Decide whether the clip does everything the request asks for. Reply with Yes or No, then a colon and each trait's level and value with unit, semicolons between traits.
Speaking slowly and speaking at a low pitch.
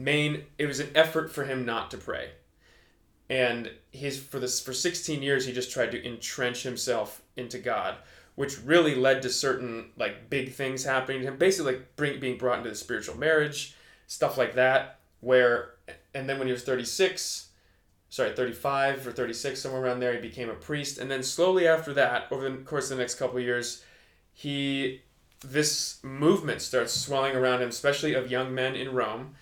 No: average, 190 wpm; low, 130 Hz